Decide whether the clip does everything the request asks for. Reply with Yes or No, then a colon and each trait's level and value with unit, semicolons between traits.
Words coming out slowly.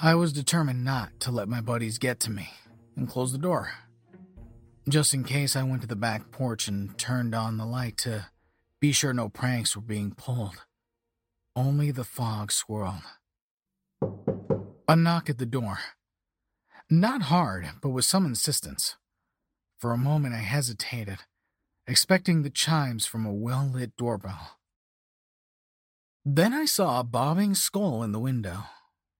No: average, 150 wpm